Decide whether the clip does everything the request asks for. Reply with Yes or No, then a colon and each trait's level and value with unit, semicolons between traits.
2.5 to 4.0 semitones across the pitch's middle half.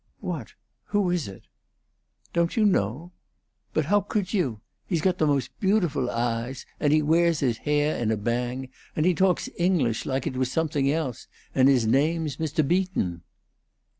No: average, 5.3 semitones